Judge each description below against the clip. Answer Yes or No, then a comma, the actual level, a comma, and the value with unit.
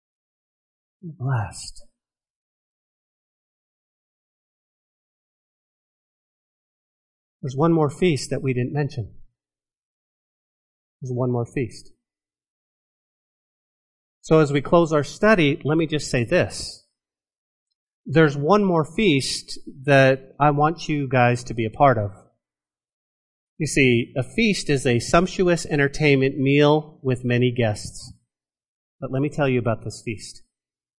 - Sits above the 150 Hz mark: No, low, 135 Hz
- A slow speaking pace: Yes, slow, 110 wpm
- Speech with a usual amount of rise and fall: Yes, average, 4.8 semitones